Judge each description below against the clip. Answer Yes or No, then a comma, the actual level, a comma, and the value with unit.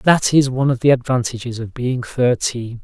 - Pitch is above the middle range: No, low, 125 Hz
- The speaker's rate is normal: Yes, average, 190 wpm